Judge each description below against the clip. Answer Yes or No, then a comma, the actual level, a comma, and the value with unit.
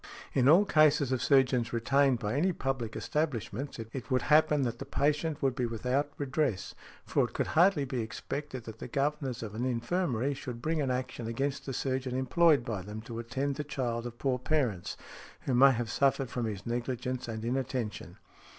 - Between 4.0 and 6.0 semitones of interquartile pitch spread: No, average, 3.3 semitones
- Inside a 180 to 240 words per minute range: Yes, average, 185 wpm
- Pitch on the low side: Yes, low, 130 Hz